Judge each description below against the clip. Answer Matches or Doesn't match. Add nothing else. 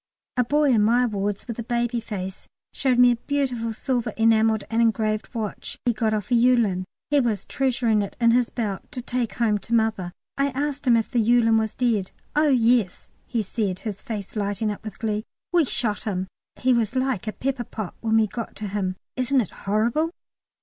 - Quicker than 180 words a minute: Matches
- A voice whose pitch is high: Matches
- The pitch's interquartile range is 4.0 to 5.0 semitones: Doesn't match